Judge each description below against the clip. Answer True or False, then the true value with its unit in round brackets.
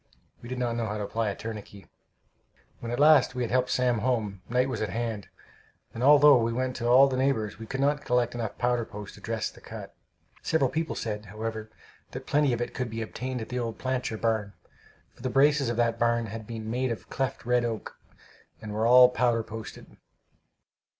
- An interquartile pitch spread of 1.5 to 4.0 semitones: True (2.4 semitones)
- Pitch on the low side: True (120 Hz)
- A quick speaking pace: True (210 wpm)